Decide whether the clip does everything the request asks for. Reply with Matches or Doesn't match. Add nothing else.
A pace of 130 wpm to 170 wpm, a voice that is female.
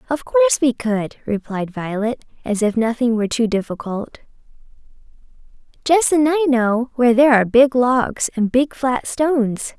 Matches